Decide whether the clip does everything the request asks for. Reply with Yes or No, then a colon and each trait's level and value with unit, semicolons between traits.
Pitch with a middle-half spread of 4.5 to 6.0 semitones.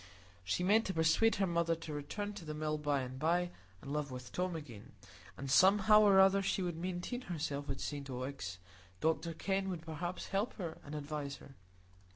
Yes: average, 4.9 semitones